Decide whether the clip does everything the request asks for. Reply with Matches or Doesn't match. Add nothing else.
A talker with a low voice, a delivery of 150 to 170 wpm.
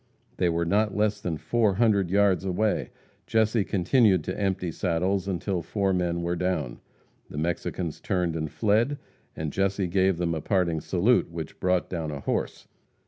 Matches